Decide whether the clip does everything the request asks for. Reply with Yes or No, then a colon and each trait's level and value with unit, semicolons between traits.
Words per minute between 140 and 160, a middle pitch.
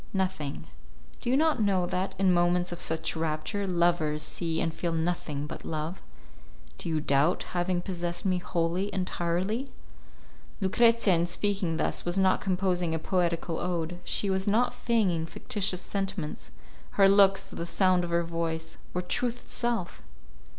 Yes: average, 150 wpm; medium, 180 Hz